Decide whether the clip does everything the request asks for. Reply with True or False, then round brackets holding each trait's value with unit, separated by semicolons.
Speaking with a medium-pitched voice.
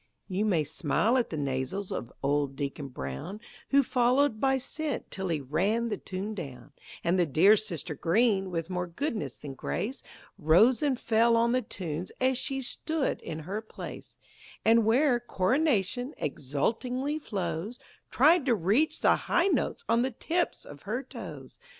False (210 Hz)